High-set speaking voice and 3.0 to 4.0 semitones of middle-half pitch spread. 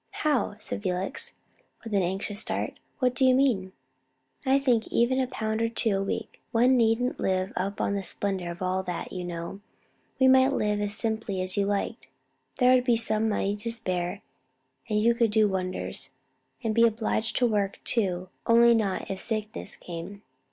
Yes: high, 215 Hz; average, 3.5 semitones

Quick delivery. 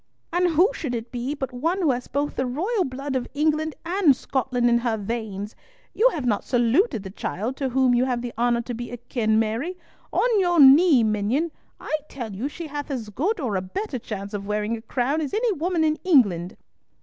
Yes: fast, 210 wpm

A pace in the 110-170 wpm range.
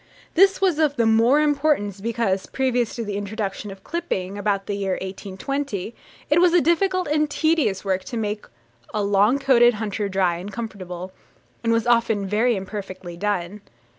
Yes: average, 165 wpm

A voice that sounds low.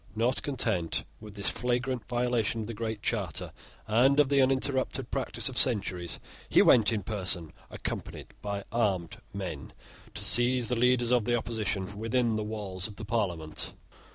Yes: low, 115 Hz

